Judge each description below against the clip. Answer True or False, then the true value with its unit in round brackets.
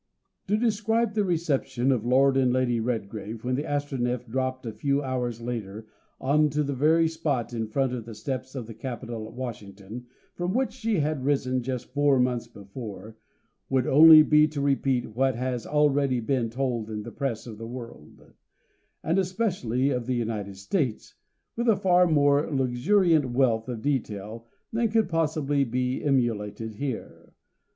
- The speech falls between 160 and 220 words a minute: True (165 wpm)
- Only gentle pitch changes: False (4.2 semitones)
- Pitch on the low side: True (130 Hz)